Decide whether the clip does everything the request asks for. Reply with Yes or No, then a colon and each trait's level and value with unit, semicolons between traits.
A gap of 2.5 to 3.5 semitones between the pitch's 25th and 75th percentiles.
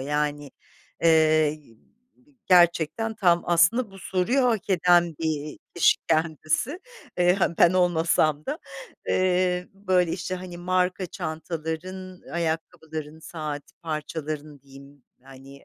Yes: average, 2.9 semitones